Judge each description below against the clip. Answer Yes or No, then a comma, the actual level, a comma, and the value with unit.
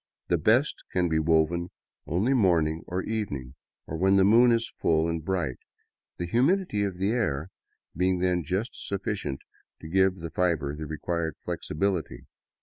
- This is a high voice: No, very low, 90 Hz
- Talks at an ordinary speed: Yes, average, 155 wpm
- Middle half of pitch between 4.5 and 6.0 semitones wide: No, average, 3.8 semitones